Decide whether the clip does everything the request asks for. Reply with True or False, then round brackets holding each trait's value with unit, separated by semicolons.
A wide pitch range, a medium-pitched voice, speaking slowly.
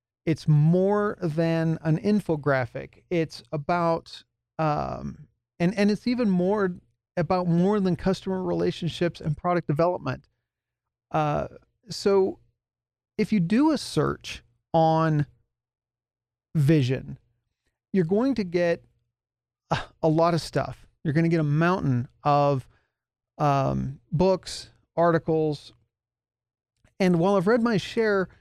True (7.1 semitones; 160 Hz; 115 wpm)